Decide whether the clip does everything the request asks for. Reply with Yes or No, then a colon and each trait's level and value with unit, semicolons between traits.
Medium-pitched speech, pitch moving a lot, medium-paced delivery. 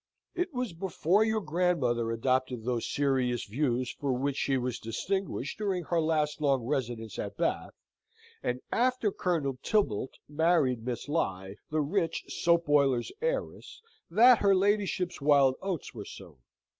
Yes: medium, 145 Hz; wide, 6.5 semitones; average, 145 wpm